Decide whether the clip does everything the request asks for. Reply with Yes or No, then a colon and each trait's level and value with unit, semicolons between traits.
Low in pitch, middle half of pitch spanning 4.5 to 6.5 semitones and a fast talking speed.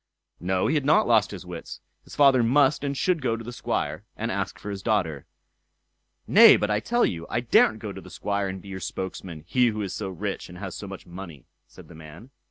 Yes: low, 100 Hz; average, 4.9 semitones; fast, 235 wpm